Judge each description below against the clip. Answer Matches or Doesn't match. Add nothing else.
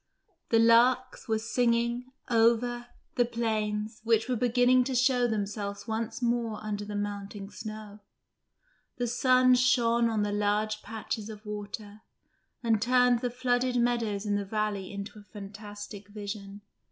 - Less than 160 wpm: Matches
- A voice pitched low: Doesn't match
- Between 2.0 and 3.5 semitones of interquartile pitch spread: Matches